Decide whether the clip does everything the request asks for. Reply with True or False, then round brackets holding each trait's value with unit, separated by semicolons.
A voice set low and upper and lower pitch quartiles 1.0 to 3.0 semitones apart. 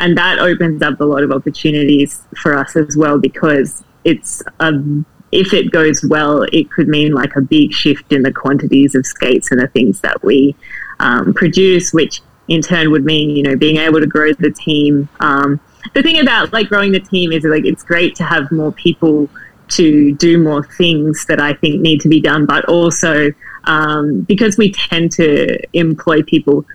False (155 Hz; 2.6 semitones)